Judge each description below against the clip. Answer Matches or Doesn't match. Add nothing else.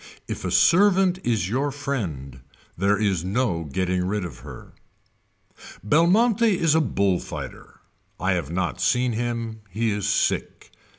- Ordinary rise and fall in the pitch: Doesn't match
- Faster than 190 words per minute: Doesn't match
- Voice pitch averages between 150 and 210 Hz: Doesn't match